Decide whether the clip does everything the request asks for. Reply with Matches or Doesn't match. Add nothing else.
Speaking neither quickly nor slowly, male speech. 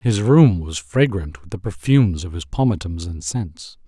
Matches